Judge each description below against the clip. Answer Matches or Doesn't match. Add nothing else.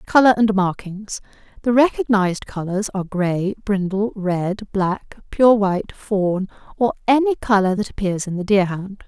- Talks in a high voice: Matches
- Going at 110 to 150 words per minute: Matches